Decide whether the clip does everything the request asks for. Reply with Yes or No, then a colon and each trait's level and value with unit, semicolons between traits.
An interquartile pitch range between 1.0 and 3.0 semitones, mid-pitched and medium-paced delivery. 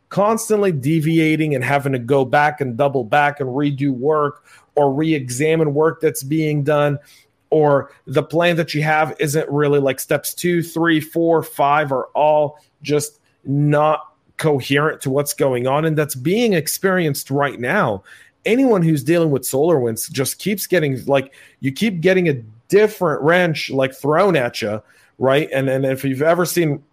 Yes: narrow, 2.6 semitones; medium, 150 Hz; average, 170 wpm